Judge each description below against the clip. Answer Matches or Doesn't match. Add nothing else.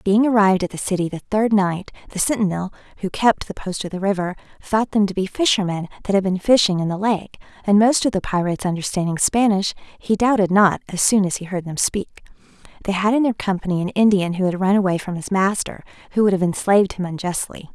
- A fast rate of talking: Matches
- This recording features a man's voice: Doesn't match